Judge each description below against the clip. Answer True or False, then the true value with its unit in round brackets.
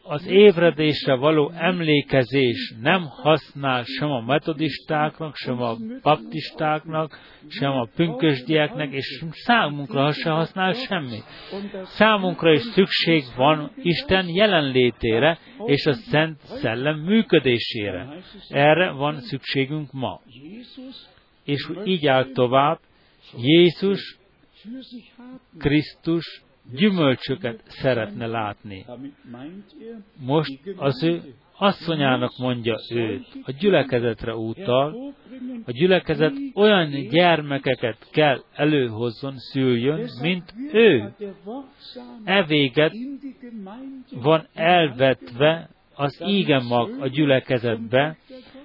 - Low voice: False (155 Hz)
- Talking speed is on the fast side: False (85 wpm)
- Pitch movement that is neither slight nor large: False (5.8 semitones)